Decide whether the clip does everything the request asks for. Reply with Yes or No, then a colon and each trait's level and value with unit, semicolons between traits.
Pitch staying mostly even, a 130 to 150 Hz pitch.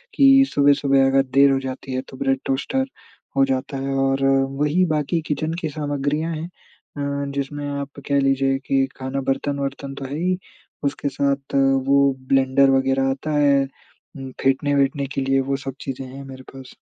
Yes: narrow, 1.1 semitones; medium, 140 Hz